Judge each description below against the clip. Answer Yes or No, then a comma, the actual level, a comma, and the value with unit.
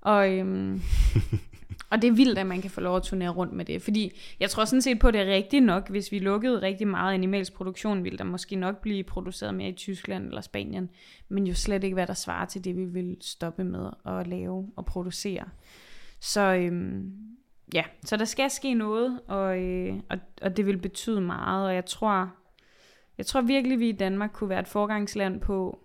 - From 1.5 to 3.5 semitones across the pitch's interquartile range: Yes, narrow, 2.4 semitones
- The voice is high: Yes, high, 195 Hz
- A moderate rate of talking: Yes, average, 215 wpm